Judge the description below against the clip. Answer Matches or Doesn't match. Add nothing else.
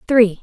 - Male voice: Doesn't match